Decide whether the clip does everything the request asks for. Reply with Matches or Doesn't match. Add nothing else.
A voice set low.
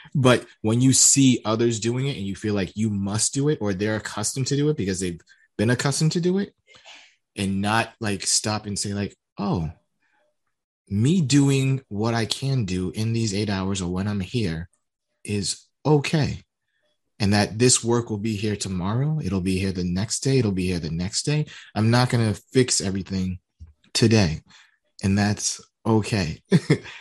Matches